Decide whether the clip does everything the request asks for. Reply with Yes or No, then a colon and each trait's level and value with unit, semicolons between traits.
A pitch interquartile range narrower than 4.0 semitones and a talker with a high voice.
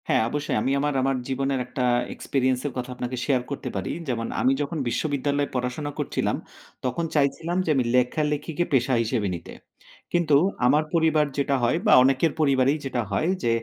No: average, 2.8 semitones; low, 135 Hz